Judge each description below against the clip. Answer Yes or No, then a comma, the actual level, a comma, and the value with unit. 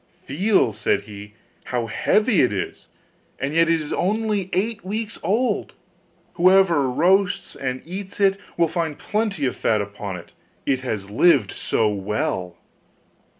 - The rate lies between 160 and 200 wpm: No, average, 145 wpm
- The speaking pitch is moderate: Yes, medium, 160 Hz